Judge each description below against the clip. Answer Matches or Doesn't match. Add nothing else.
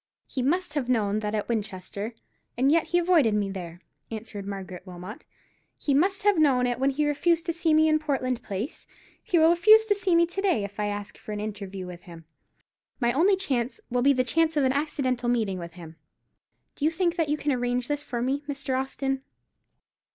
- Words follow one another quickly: Matches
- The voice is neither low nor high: Doesn't match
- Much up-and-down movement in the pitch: Matches